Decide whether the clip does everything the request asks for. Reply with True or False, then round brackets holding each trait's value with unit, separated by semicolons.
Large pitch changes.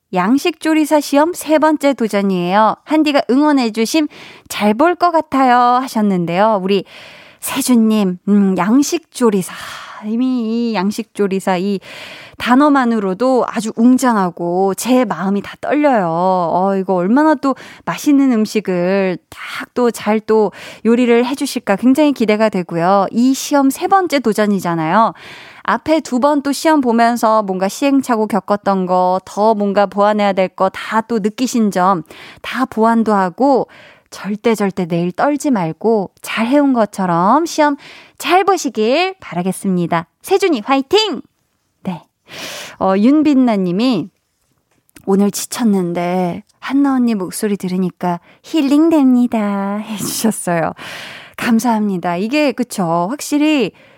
True (5.8 semitones)